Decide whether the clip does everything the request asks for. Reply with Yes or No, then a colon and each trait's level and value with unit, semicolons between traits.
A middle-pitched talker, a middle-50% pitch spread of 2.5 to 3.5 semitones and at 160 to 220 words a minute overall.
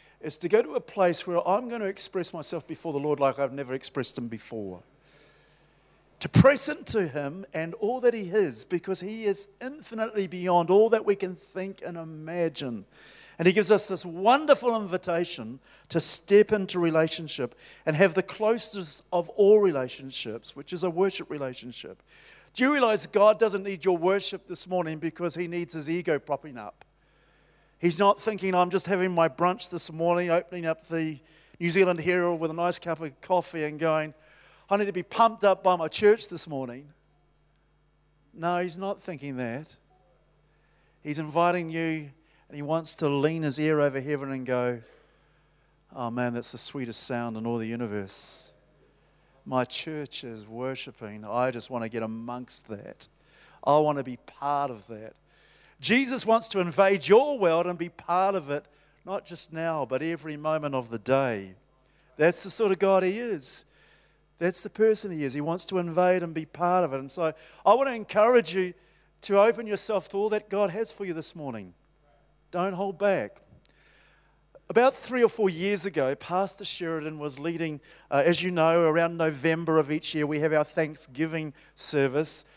No: medium, 170 Hz; average, 4.8 semitones; average, 180 wpm